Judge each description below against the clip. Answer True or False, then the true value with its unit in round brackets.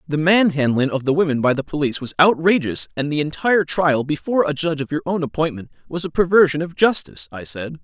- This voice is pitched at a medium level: True (155 Hz)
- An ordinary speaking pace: False (215 wpm)